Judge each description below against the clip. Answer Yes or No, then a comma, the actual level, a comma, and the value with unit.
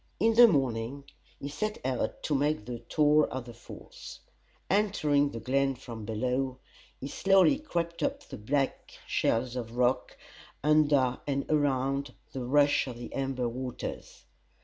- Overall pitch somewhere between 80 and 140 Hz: Yes, low, 135 Hz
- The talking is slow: No, average, 150 wpm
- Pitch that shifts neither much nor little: Yes, average, 3.2 semitones